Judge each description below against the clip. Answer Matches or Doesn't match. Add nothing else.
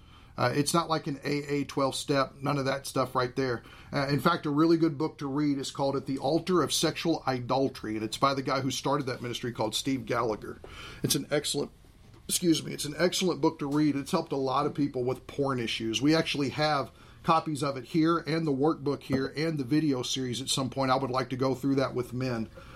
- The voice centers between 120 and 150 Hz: Matches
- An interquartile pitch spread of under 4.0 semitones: Matches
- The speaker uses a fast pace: Matches